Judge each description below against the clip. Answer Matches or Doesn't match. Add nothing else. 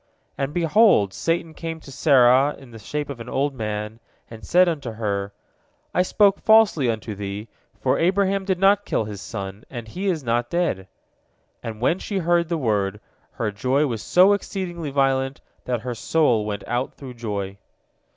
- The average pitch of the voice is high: Doesn't match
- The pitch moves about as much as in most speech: Doesn't match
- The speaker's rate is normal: Matches